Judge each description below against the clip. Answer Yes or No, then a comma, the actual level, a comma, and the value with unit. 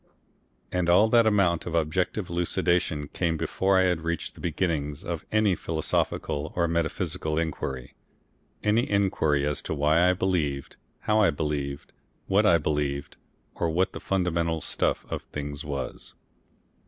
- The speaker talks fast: No, average, 145 wpm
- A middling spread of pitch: Yes, average, 3.6 semitones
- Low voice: Yes, very low, 85 Hz